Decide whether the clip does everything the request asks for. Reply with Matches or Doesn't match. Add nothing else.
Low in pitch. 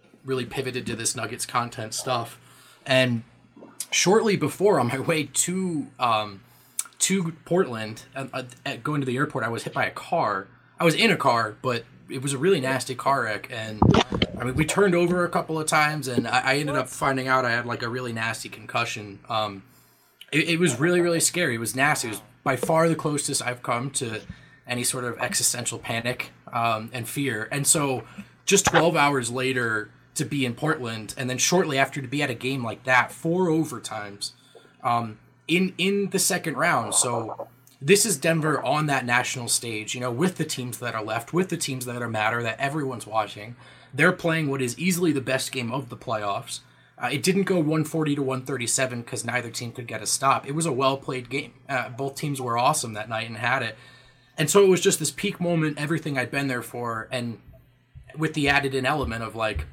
Matches